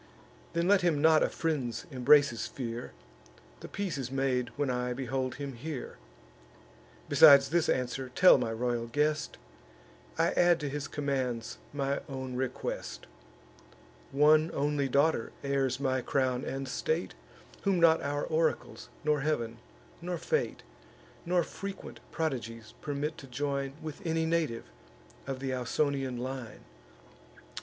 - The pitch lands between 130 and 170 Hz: Yes, medium, 140 Hz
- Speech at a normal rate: No, slow, 130 wpm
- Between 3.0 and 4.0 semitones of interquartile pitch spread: Yes, average, 3.4 semitones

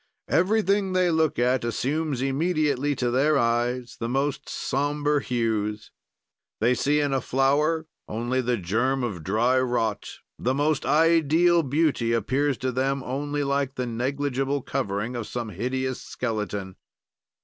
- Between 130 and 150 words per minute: Yes, average, 140 wpm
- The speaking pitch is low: Yes, low, 130 Hz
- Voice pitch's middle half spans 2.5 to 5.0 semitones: Yes, average, 3.4 semitones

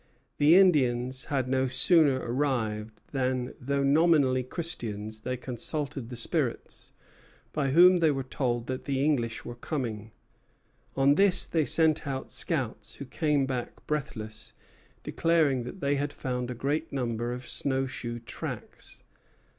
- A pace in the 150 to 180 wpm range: No, average, 140 wpm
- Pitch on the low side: Yes, low, 130 Hz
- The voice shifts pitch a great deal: No, average, 3.4 semitones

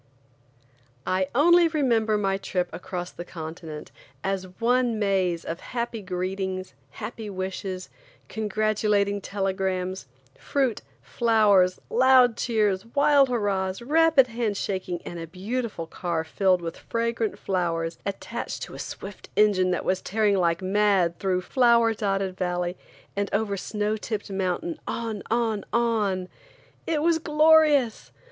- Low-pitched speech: No, high, 200 Hz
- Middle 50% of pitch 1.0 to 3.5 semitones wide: No, average, 3.9 semitones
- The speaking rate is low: Yes, slow, 125 wpm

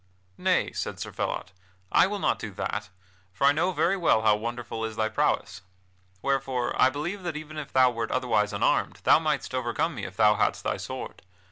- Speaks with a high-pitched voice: No, low, 125 Hz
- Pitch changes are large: Yes, wide, 5.7 semitones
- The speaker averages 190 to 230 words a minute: Yes, average, 200 wpm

